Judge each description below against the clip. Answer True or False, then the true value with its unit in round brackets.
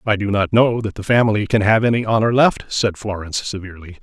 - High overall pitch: False (105 Hz)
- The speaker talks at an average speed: False (225 wpm)